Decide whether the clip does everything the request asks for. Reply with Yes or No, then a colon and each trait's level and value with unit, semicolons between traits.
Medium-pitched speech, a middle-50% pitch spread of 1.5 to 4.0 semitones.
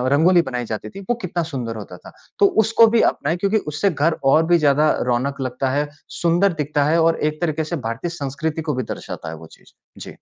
No: medium, 155 Hz; average, 4.6 semitones